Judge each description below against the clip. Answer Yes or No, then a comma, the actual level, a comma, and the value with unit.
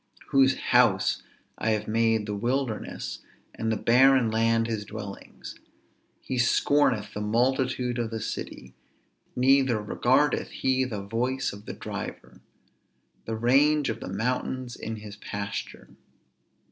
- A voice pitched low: Yes, low, 115 Hz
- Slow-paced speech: Yes, slow, 130 wpm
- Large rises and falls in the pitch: No, average, 3.3 semitones